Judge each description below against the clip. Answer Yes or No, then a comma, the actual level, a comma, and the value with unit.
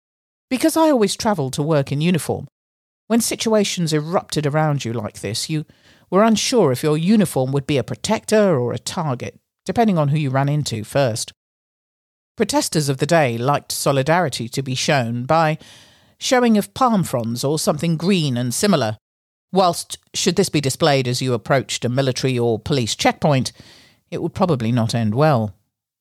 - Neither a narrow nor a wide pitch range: No, wide, 6.9 semitones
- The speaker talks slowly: No, average, 170 wpm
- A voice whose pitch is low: No, medium, 145 Hz